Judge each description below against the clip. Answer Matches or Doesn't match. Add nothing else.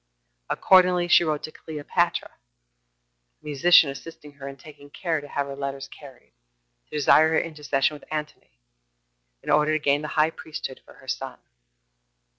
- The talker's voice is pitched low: Doesn't match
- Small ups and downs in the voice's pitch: Matches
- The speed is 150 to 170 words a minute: Matches